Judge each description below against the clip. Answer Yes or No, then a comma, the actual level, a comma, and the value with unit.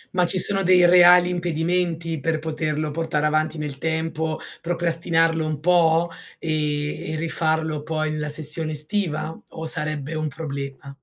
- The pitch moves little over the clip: Yes, narrow, 1.7 semitones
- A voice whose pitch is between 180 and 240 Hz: No, medium, 160 Hz